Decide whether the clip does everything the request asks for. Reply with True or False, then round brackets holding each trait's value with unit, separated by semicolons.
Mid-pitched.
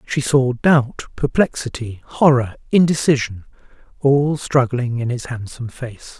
False (130 Hz)